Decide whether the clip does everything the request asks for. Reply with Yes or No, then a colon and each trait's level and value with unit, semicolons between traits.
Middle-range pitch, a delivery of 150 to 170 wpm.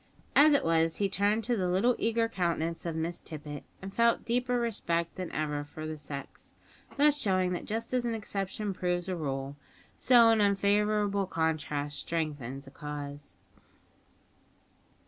Yes: medium, 180 Hz; average, 155 wpm